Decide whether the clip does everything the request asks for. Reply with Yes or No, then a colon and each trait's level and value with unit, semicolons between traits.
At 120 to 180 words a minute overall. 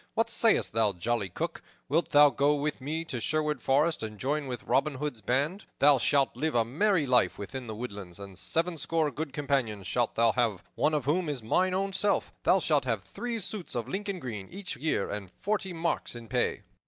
No: fast, 205 wpm